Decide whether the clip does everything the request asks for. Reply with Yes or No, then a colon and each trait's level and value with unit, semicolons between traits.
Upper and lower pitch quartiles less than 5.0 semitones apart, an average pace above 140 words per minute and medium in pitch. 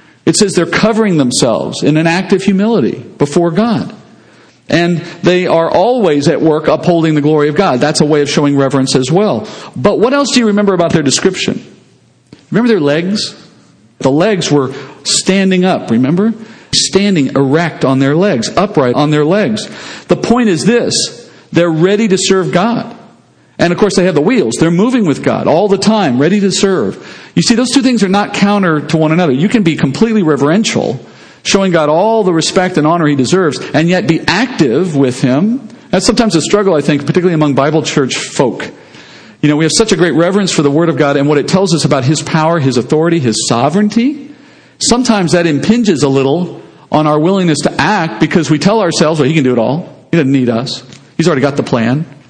No: wide, 5.4 semitones; fast, 205 wpm; medium, 170 Hz